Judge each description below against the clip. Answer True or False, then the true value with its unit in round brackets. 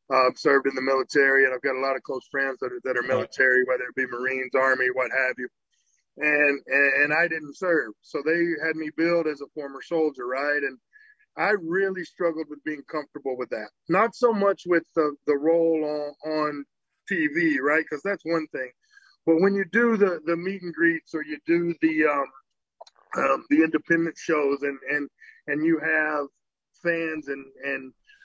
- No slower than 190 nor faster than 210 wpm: True (200 wpm)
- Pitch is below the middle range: False (155 Hz)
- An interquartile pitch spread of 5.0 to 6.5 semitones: False (3.7 semitones)